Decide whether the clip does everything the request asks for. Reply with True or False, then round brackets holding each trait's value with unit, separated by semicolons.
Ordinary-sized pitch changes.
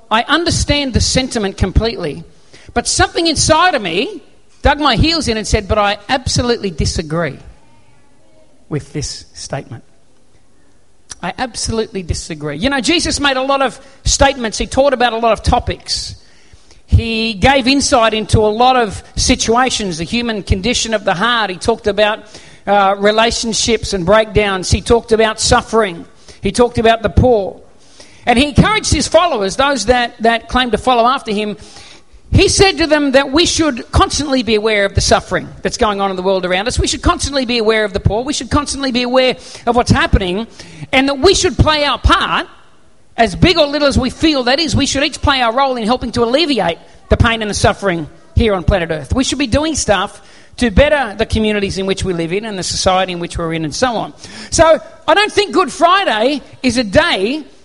True (4.8 semitones)